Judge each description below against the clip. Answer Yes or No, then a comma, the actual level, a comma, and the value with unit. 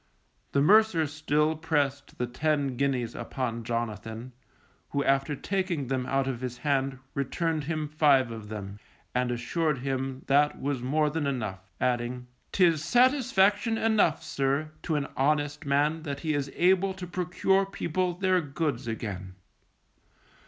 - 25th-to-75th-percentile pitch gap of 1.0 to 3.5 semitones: No, average, 4.1 semitones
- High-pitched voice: No, medium, 145 Hz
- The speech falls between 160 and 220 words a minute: No, average, 145 wpm